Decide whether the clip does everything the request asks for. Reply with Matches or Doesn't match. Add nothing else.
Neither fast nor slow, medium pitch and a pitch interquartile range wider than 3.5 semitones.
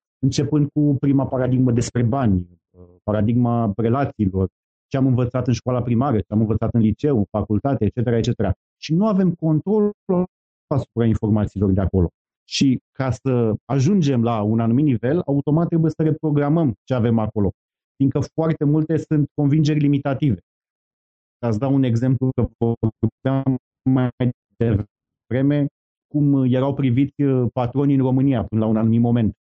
Doesn't match